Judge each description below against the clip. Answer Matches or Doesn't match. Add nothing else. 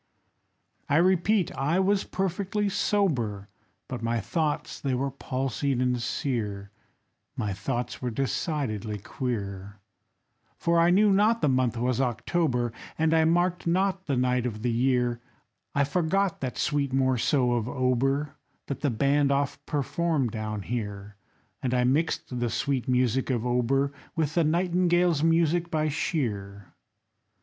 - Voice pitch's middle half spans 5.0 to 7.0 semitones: Matches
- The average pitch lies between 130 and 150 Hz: Matches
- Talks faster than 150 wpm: Doesn't match